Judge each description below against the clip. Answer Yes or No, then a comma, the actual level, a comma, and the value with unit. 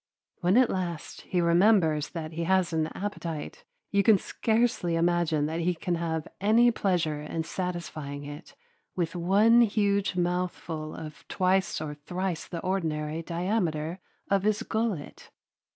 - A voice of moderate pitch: Yes, medium, 175 Hz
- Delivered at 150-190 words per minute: No, average, 140 wpm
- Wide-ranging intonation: No, average, 3.3 semitones